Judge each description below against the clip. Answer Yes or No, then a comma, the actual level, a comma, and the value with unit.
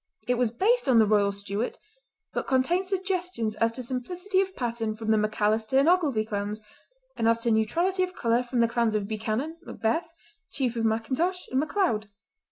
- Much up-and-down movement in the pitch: Yes, wide, 7.6 semitones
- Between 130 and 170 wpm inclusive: No, average, 180 wpm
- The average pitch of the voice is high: Yes, high, 235 Hz